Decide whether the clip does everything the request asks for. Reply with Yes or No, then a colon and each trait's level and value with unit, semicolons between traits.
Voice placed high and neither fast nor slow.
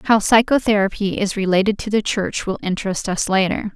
Yes: high, 200 Hz; average, 175 wpm